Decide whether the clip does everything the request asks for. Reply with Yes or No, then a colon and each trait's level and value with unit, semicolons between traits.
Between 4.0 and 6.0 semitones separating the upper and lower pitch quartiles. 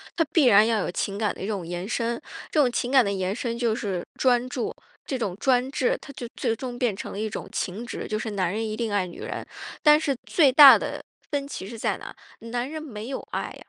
Yes: average, 4.3 semitones